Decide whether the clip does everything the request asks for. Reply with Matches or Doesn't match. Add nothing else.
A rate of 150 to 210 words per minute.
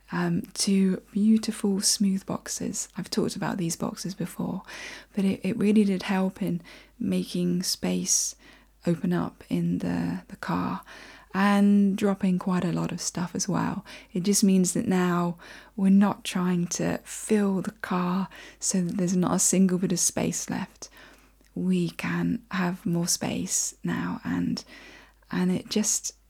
Matches